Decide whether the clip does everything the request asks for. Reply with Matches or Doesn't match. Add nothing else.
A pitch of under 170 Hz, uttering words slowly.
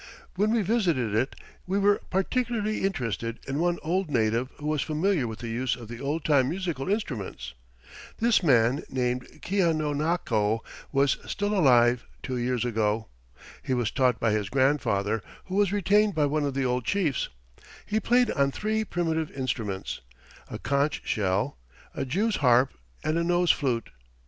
Doesn't match